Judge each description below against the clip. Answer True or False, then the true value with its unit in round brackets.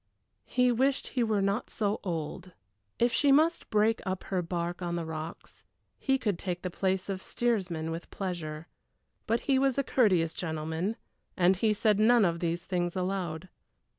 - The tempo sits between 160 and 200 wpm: True (170 wpm)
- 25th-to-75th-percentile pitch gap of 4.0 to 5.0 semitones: True (4.7 semitones)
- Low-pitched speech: False (190 Hz)